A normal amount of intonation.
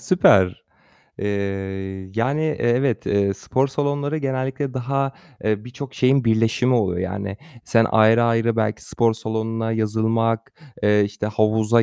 Yes: average, 3.2 semitones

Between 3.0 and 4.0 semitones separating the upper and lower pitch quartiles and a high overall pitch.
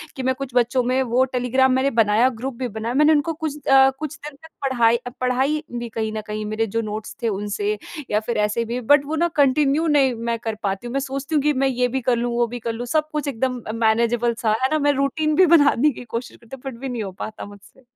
Yes: average, 3.3 semitones; very high, 250 Hz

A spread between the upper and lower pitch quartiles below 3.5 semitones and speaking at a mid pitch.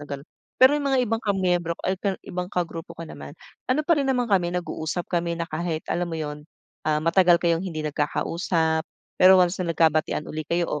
Yes: average, 2.8 semitones; medium, 170 Hz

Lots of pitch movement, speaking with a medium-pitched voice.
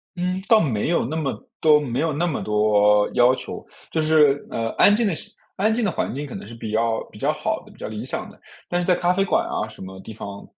Yes: wide, 8.1 semitones; medium, 145 Hz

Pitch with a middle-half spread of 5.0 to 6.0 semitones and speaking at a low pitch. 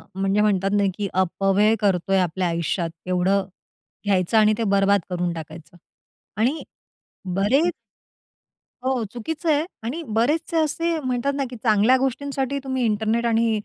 No: average, 5.3 semitones; high, 215 Hz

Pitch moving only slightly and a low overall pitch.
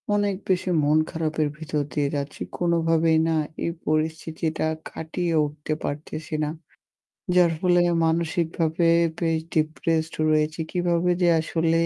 No: narrow, 1.5 semitones; medium, 160 Hz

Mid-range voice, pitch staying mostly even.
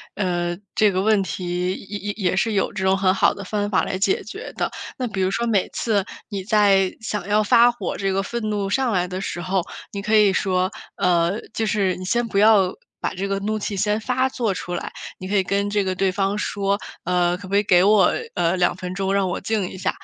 No: high, 195 Hz; narrow, 2.2 semitones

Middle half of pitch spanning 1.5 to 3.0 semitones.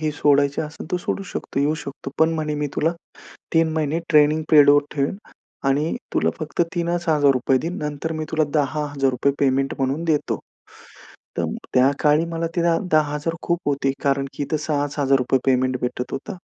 Yes: narrow, 2.5 semitones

